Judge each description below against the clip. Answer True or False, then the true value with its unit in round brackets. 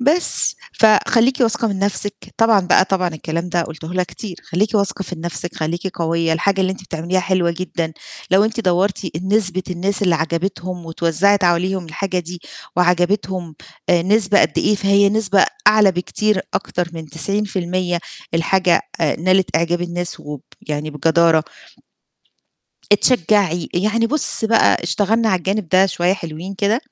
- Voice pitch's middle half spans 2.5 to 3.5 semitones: True (2.9 semitones)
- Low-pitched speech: False (185 Hz)